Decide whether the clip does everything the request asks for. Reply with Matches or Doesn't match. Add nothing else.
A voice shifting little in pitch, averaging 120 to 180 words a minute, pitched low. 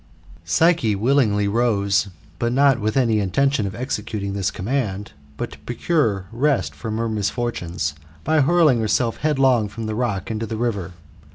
Doesn't match